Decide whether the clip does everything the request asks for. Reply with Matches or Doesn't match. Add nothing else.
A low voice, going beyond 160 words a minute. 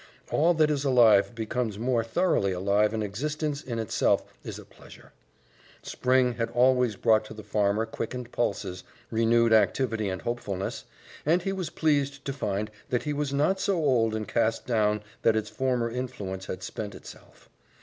Matches